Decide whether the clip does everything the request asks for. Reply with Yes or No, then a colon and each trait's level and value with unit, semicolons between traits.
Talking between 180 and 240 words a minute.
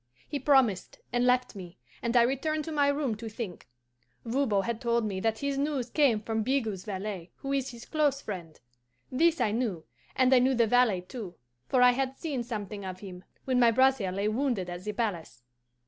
Yes: average, 200 wpm